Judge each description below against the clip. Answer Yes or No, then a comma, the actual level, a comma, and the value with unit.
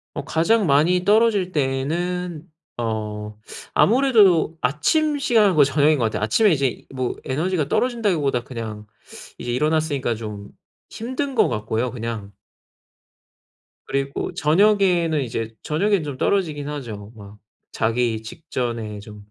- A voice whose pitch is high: No, medium, 145 Hz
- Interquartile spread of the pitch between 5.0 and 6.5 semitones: No, wide, 7.7 semitones